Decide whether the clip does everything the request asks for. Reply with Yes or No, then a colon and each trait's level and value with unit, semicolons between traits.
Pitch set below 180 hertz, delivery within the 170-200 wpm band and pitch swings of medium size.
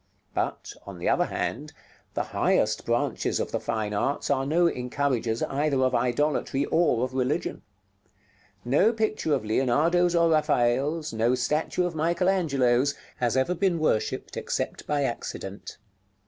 No: medium, 140 Hz; average, 145 wpm; average, 4.9 semitones